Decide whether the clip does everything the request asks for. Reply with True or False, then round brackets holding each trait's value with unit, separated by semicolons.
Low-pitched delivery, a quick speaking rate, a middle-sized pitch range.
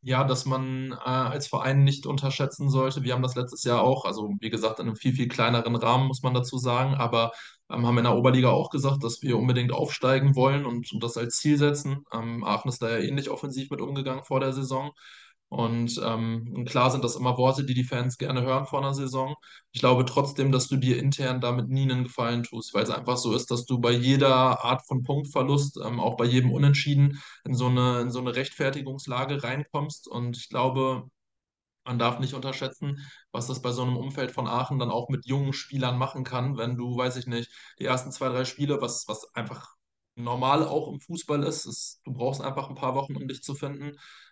False (130 Hz; 220 wpm; 1.9 semitones)